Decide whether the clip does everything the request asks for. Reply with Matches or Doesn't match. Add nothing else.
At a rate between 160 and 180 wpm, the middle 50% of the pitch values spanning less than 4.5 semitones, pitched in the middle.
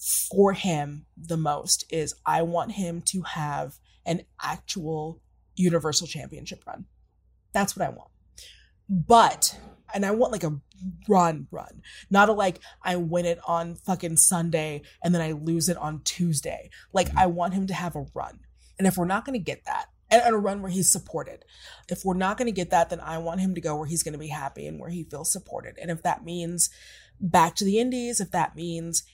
Doesn't match